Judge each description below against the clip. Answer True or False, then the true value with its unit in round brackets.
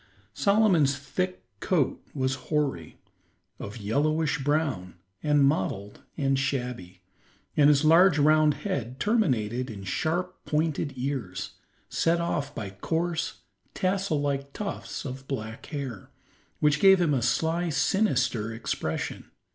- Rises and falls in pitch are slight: False (4.6 semitones)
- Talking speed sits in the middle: False (125 wpm)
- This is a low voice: False (145 Hz)